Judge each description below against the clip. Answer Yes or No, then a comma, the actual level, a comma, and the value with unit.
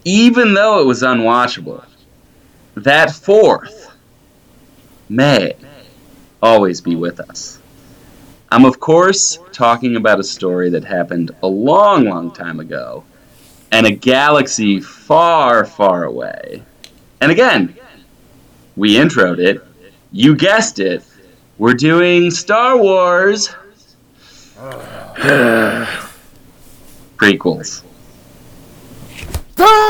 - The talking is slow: Yes, slow, 90 wpm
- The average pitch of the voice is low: Yes, low, 130 Hz